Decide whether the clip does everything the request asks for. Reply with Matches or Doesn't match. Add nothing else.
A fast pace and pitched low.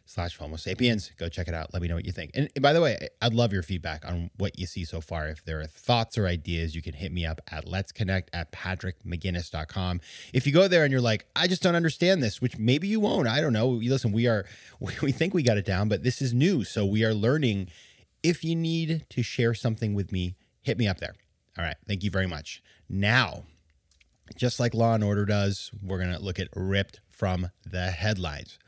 Matches